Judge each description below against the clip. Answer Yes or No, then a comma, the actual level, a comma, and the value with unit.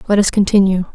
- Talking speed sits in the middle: Yes, average, 190 wpm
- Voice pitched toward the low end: No, high, 195 Hz